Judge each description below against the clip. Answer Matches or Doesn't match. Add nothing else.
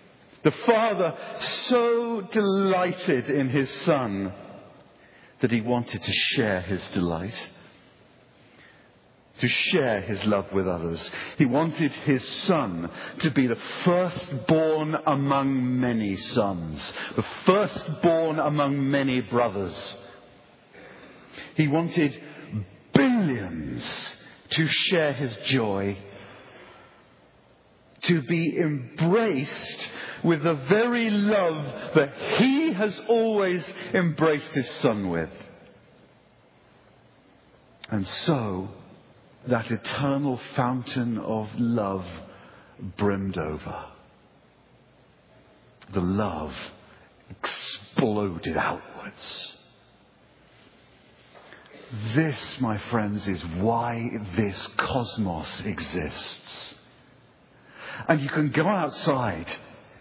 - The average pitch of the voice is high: Doesn't match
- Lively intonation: Matches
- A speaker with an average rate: Doesn't match